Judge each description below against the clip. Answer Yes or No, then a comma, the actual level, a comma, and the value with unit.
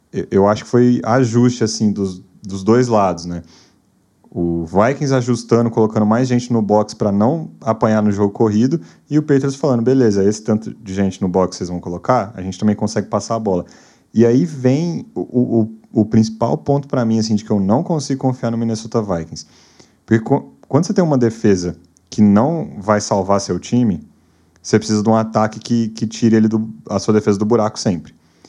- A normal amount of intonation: Yes, average, 3.2 semitones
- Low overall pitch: Yes, low, 110 Hz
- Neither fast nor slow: No, fast, 200 wpm